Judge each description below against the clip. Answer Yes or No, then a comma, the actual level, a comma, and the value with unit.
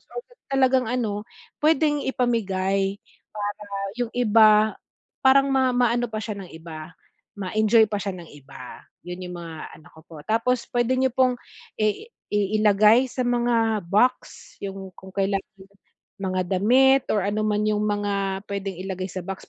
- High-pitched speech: Yes, high, 210 Hz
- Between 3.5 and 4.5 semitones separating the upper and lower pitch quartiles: Yes, average, 4.0 semitones